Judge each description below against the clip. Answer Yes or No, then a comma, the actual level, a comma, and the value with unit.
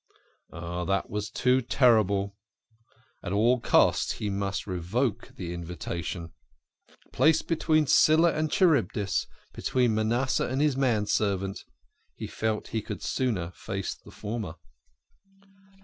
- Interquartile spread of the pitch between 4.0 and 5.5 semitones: Yes, average, 4.8 semitones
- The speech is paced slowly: Yes, slow, 125 wpm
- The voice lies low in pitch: Yes, low, 105 Hz